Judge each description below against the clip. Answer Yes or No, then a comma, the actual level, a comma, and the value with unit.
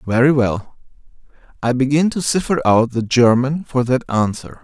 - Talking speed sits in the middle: Yes, average, 155 wpm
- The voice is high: No, low, 130 Hz